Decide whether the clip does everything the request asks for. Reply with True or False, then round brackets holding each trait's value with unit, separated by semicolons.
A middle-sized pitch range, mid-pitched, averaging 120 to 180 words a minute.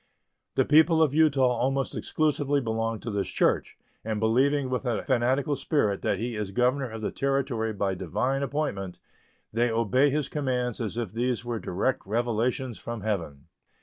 False (3.7 semitones; 120 Hz; 165 wpm)